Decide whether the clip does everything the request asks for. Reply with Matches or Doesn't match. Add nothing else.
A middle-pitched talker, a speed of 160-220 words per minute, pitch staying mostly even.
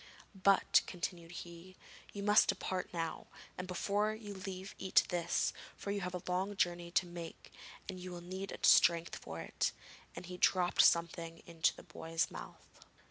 Matches